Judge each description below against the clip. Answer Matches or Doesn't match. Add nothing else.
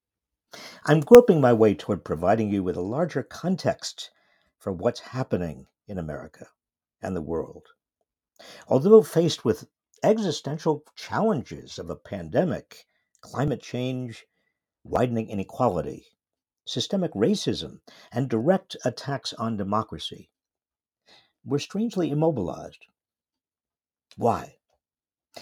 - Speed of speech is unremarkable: Doesn't match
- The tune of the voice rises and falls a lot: Matches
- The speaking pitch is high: Doesn't match